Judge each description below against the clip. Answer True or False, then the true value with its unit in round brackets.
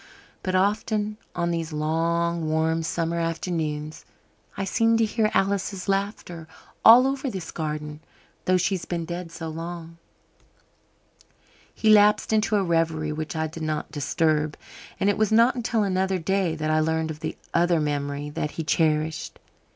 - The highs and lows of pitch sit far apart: False (3.8 semitones)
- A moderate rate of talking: True (155 wpm)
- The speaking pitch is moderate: True (170 Hz)